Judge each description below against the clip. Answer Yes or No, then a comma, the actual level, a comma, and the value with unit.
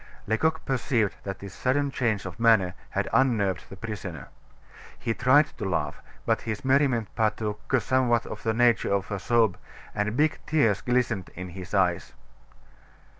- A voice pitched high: No, low, 110 Hz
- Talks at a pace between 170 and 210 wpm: No, average, 155 wpm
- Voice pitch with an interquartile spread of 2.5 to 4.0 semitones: No, average, 4.4 semitones